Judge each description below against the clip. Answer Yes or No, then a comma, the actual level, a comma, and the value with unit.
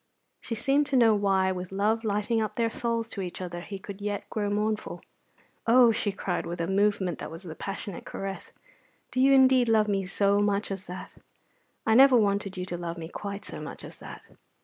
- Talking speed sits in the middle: No, fast, 210 wpm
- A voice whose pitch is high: Yes, high, 205 Hz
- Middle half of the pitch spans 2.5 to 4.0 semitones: Yes, average, 2.9 semitones